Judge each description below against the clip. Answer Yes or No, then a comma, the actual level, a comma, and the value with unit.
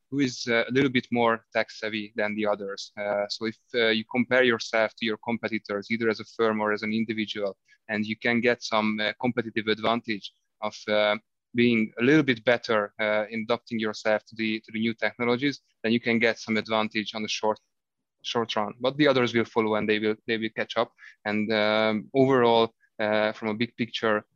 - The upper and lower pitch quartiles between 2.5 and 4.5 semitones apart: No, narrow, 1.8 semitones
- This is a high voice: No, low, 110 Hz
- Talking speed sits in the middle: No, fast, 210 wpm